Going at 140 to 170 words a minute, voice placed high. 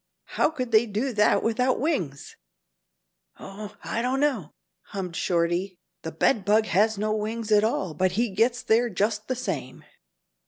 Yes: average, 160 wpm; high, 215 Hz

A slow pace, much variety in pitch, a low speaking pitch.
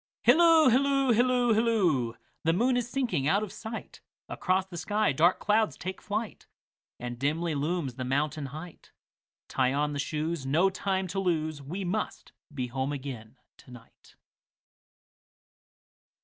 No: slow, 125 wpm; wide, 7.4 semitones; medium, 175 Hz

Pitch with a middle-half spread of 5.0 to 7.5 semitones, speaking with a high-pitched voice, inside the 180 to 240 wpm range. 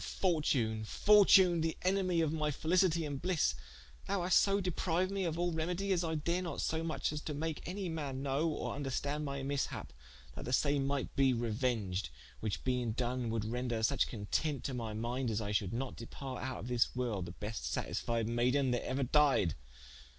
No: wide, 5.5 semitones; medium, 140 Hz; average, 190 wpm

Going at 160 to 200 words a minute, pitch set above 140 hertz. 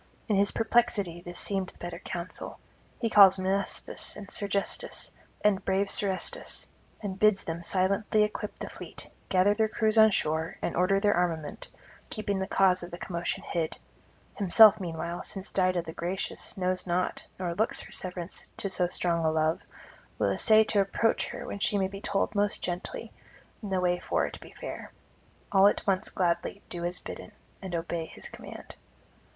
Yes: average, 175 wpm; high, 190 Hz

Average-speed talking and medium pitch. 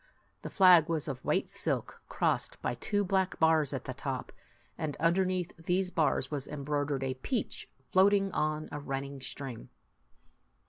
Yes: average, 155 wpm; medium, 155 Hz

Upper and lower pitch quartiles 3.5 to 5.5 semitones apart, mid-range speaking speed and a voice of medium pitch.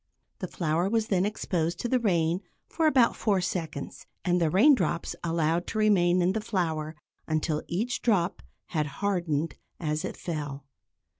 Yes: average, 4.3 semitones; average, 155 wpm; medium, 175 Hz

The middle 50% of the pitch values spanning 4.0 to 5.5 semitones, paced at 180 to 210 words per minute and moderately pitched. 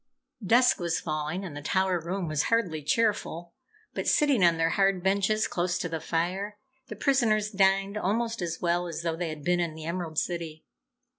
No: average, 3.5 semitones; average, 190 wpm; medium, 180 Hz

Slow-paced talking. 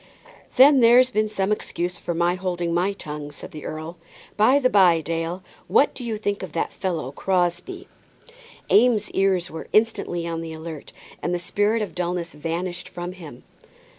No: average, 170 wpm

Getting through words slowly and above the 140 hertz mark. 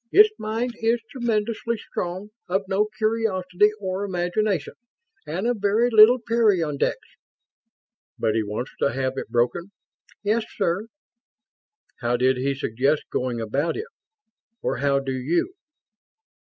Yes: slow, 130 wpm; high, 190 Hz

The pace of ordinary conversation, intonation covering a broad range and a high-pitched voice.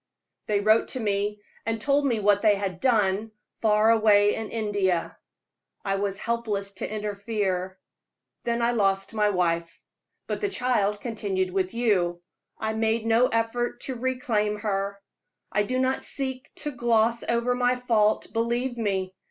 No: average, 150 wpm; average, 2.8 semitones; high, 215 Hz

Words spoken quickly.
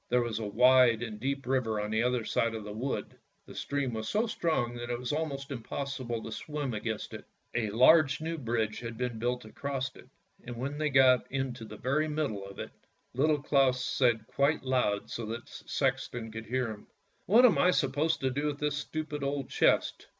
Yes: fast, 210 wpm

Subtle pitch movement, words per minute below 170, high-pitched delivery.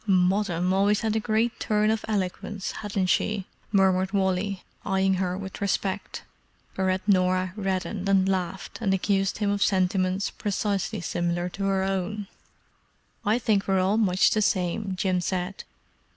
Yes: narrow, 1.8 semitones; average, 150 wpm; high, 195 Hz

